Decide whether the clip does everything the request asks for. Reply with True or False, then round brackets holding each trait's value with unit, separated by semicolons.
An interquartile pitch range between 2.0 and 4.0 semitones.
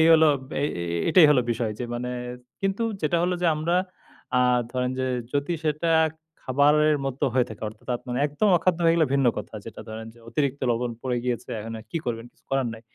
False (4.7 semitones)